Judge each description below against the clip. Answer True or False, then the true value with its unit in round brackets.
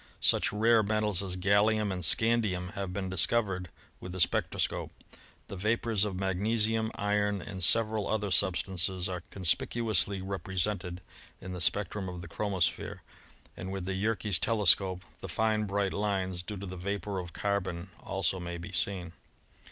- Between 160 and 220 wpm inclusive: False (150 wpm)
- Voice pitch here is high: False (95 Hz)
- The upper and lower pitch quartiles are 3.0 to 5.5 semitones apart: False (2.4 semitones)